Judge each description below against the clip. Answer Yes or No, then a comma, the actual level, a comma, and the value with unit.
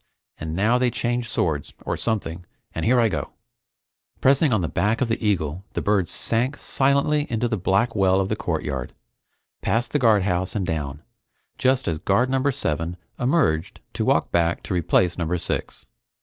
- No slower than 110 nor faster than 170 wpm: No, average, 180 wpm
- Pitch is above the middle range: No, low, 105 Hz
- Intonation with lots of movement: Yes, wide, 6.0 semitones